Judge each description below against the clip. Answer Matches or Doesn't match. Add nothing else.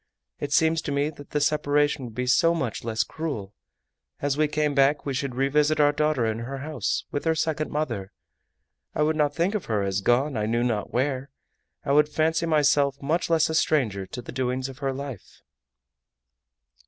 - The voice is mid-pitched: Matches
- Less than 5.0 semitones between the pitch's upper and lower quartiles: Matches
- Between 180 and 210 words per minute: Matches